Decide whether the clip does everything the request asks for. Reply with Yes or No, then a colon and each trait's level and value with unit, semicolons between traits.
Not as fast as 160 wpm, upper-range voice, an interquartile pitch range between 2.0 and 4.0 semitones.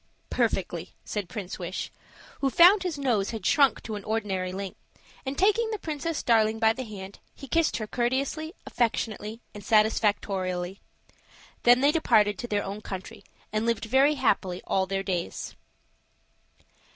No: average, 150 wpm; high, 220 Hz; wide, 5.4 semitones